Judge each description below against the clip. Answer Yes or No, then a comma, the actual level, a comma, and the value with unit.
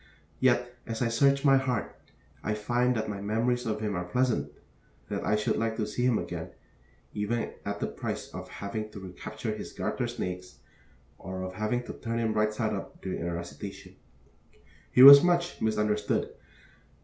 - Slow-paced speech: No, average, 175 wpm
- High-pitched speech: No, low, 110 Hz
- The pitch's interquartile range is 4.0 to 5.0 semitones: No, average, 3.2 semitones